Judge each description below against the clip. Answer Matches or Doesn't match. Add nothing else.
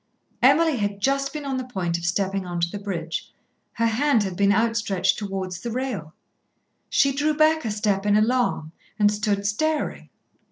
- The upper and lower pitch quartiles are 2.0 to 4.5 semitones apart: Doesn't match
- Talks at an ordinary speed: Matches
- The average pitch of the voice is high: Matches